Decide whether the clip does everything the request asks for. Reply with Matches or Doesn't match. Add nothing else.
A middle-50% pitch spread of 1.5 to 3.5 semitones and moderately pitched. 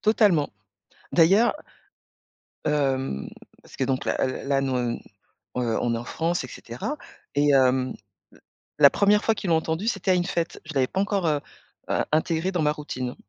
Doesn't match